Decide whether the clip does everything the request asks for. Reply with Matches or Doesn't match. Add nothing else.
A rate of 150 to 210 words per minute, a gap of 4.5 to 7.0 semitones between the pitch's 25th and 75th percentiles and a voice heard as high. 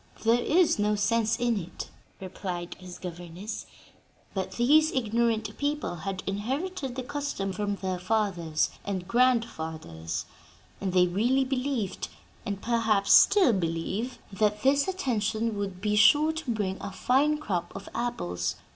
Doesn't match